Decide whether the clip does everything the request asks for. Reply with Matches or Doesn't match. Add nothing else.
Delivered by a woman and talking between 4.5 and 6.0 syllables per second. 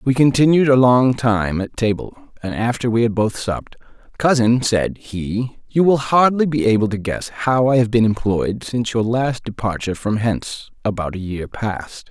Doesn't match